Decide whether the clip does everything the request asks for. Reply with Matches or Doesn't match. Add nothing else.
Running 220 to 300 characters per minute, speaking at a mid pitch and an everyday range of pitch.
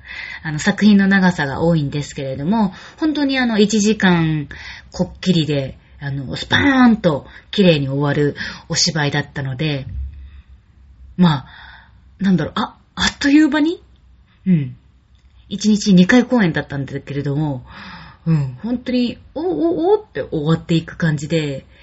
Doesn't match